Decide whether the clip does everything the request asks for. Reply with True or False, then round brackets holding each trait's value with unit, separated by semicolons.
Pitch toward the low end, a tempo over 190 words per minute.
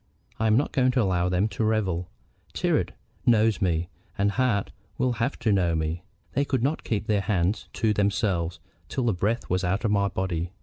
True (100 Hz; 200 wpm)